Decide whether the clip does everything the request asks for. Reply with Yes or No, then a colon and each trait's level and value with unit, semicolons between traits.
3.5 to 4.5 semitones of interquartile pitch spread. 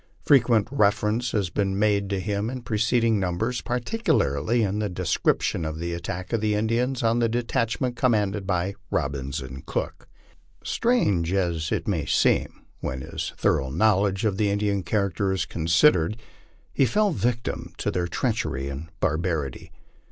No: average, 5.2 semitones